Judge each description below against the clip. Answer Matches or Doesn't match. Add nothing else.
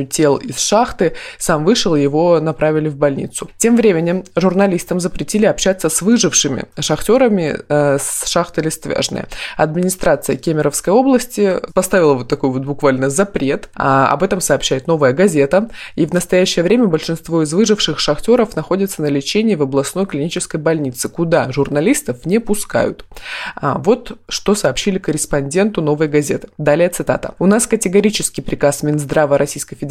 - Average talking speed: Matches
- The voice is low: Doesn't match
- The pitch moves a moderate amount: Matches